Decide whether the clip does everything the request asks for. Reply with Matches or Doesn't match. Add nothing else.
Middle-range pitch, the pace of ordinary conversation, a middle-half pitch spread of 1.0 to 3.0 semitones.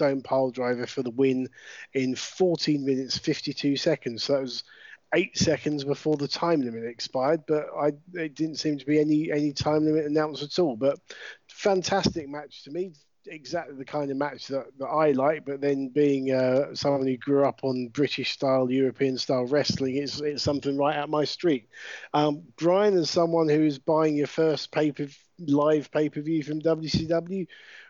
Matches